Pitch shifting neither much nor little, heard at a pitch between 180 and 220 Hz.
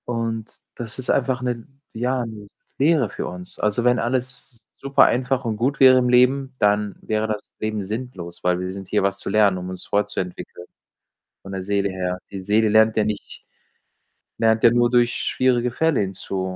No: average, 3.7 semitones; low, 110 Hz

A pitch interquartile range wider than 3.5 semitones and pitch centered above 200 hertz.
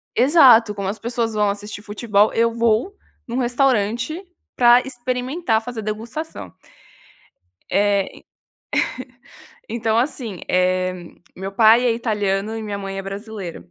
No: average, 3.1 semitones; high, 220 Hz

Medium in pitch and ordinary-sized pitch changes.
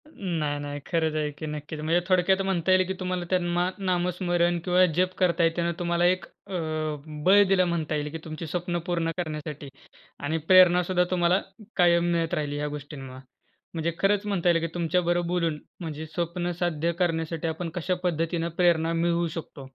No: medium, 170 Hz; narrow, 2.1 semitones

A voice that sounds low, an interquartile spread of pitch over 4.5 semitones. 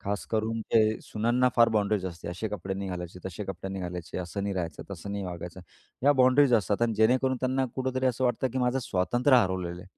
Yes: low, 105 Hz; average, 5.2 semitones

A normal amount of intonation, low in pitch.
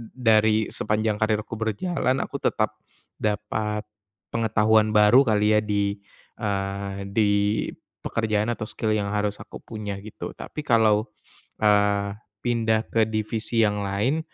No: narrow, 1.3 semitones; low, 110 Hz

